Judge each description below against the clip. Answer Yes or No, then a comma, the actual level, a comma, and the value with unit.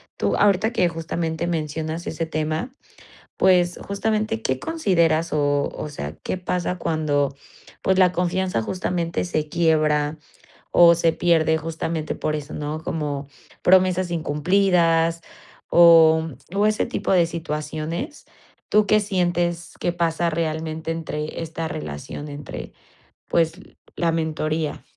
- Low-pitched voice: No, medium, 165 Hz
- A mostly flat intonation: Yes, narrow, 2.3 semitones